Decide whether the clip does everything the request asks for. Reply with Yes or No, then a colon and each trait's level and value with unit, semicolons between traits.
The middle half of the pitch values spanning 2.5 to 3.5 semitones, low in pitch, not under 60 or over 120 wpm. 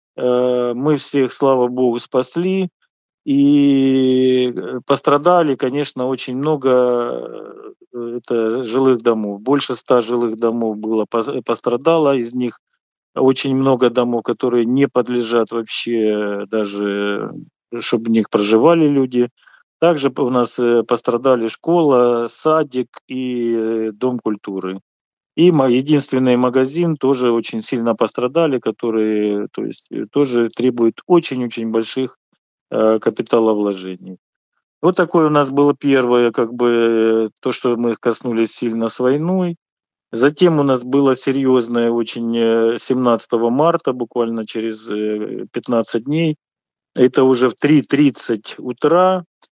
Yes: average, 3.1 semitones; low, 125 Hz; average, 110 wpm